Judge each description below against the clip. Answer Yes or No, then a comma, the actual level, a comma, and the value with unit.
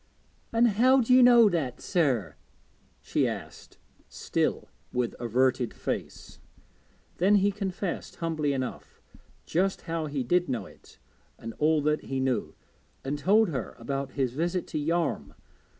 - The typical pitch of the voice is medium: Yes, medium, 155 Hz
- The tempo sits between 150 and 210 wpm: No, average, 140 wpm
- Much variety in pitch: Yes, wide, 6.5 semitones